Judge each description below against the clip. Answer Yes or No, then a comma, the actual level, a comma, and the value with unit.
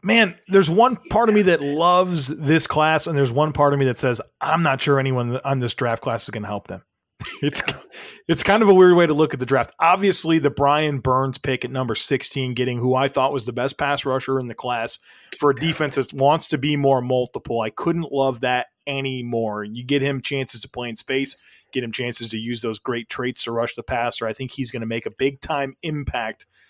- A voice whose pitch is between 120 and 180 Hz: Yes, low, 135 Hz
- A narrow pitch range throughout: No, average, 3.5 semitones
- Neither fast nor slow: No, fast, 240 wpm